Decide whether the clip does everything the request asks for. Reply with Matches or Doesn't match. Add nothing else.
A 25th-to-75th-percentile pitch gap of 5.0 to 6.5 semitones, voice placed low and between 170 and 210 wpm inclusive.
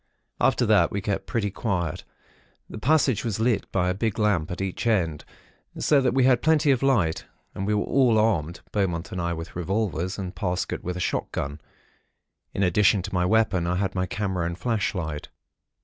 Doesn't match